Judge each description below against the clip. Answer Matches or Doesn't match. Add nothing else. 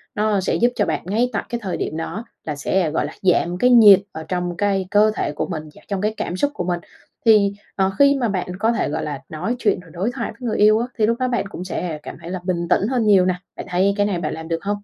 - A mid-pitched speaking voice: Doesn't match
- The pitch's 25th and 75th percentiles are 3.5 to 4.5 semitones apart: Matches